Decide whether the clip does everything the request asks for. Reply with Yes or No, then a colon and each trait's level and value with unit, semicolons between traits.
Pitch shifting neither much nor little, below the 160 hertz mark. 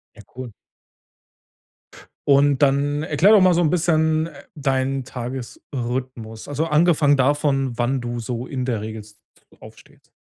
Yes: average, 3.5 semitones; low, 135 Hz